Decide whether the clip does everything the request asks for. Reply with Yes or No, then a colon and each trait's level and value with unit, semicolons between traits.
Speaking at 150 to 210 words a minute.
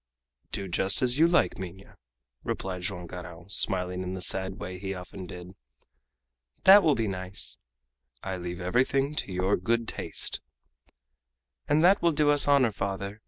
Yes: average, 160 wpm